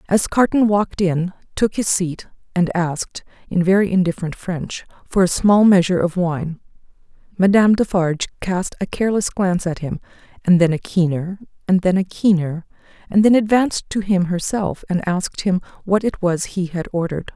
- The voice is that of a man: No, female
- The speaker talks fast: No, average, 175 wpm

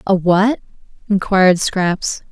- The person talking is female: Yes, female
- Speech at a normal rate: No, slow, 105 wpm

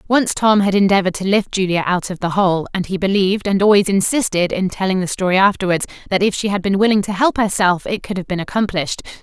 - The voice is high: Yes, high, 195 Hz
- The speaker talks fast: Yes, fast, 235 wpm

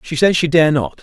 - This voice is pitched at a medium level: Yes, medium, 150 Hz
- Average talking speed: No, fast, 295 wpm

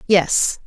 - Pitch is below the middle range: No, high, 190 Hz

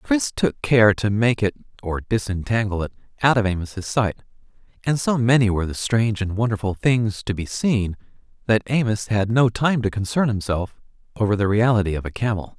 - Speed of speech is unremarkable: Yes, average, 185 wpm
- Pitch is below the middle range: Yes, low, 110 Hz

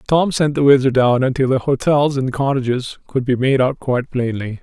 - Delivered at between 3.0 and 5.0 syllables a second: No, 5.2 syllables/s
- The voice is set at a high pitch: No, low, 130 Hz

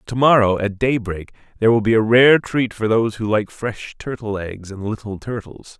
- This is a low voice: Yes, low, 110 Hz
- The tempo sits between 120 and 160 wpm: No, average, 195 wpm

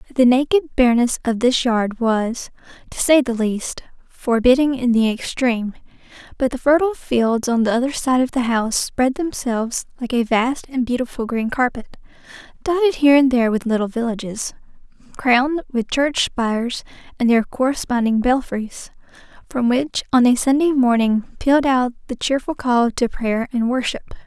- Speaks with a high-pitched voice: Yes, very high, 250 Hz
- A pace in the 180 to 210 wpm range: No, average, 160 wpm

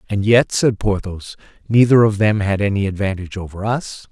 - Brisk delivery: No, average, 175 wpm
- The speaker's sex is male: Yes, male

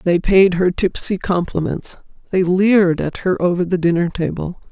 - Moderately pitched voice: Yes, medium, 180 Hz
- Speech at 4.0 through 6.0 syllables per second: Yes, 4.8 syllables/s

